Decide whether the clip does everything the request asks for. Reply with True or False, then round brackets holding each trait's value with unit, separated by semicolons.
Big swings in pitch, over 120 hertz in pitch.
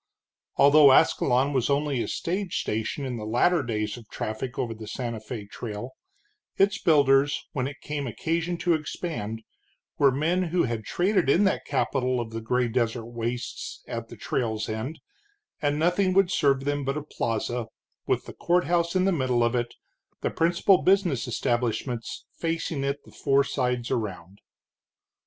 True (5.7 semitones; 135 Hz)